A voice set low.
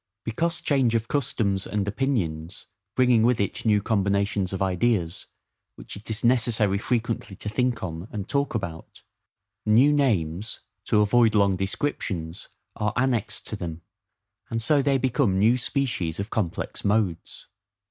Yes: low, 105 Hz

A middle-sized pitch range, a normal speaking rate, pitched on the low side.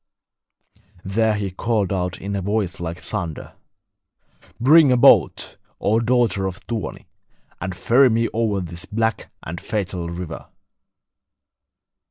No: average, 3.9 semitones; slow, 125 wpm; low, 100 Hz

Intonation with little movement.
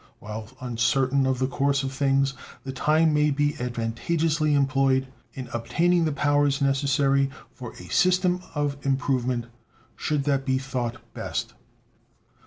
Yes: narrow, 2.2 semitones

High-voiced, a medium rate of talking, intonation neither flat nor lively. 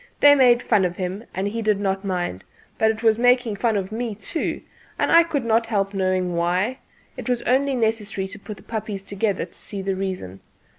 No: high, 210 Hz; fast, 210 wpm; average, 3.5 semitones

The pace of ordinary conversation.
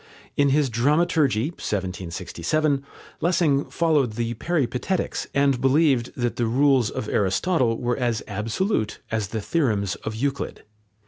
No: slow, 125 wpm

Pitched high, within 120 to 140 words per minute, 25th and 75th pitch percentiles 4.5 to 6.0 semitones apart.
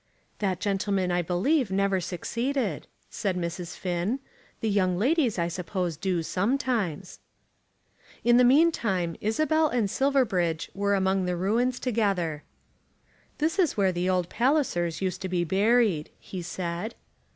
Yes: high, 195 Hz; slow, 135 wpm; average, 5.2 semitones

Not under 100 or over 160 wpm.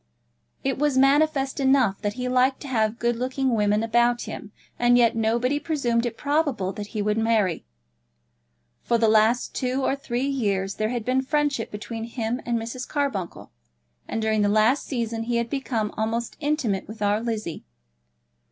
No: average, 170 wpm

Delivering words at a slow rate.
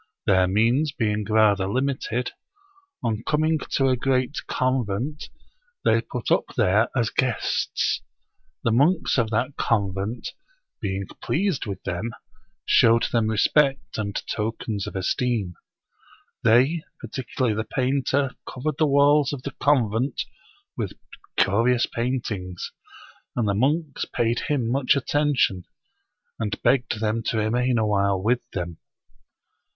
Yes: slow, 125 wpm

